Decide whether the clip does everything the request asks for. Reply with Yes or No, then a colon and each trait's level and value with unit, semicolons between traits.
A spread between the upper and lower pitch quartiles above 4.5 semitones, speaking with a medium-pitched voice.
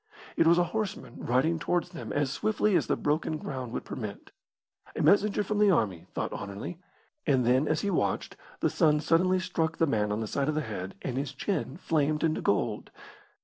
Yes: wide, 5.4 semitones; medium, 155 Hz